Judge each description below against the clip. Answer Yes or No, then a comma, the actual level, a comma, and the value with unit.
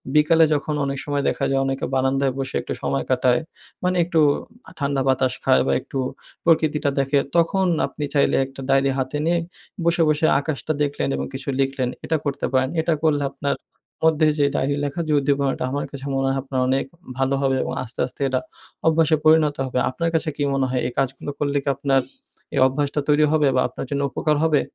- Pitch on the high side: No, medium, 140 Hz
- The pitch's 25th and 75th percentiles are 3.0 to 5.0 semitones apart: No, narrow, 2.4 semitones